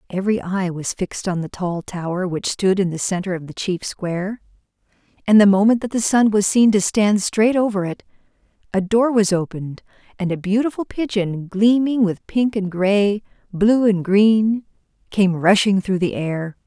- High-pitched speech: Yes, high, 200 Hz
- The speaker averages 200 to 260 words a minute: No, average, 185 wpm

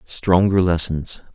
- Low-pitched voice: Yes, very low, 90 Hz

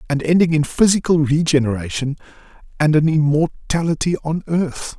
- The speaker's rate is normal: No, slow, 120 wpm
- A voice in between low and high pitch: Yes, medium, 155 Hz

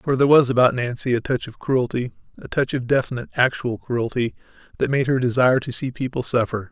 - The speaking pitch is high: No, low, 125 Hz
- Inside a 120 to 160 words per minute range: No, average, 195 wpm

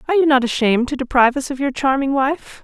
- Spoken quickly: Yes, fast, 250 wpm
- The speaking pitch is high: Yes, very high, 270 Hz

